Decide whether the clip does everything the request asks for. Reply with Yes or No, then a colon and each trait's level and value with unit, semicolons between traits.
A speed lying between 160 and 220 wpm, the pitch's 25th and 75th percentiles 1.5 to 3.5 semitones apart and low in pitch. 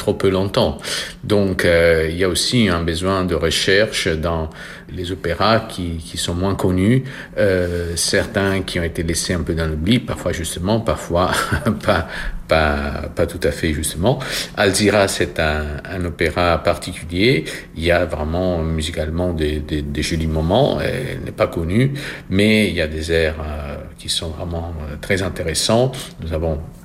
Yes: average, 170 wpm; average, 3.2 semitones; very low, 85 Hz